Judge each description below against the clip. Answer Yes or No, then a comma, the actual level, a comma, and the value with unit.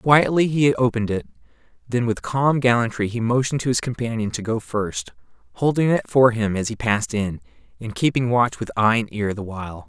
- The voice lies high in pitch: No, low, 115 Hz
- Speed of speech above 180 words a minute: Yes, average, 200 wpm